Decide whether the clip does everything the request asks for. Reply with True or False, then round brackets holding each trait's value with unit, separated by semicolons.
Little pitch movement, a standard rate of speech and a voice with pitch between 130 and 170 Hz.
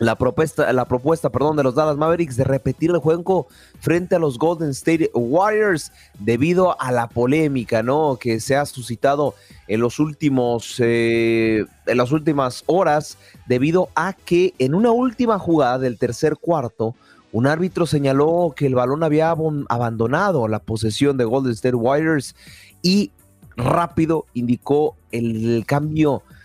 False (5.1 semitones; 145 wpm; 140 Hz)